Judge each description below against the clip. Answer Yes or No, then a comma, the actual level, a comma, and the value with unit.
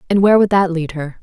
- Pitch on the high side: No, medium, 180 Hz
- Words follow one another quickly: Yes, fast, 295 wpm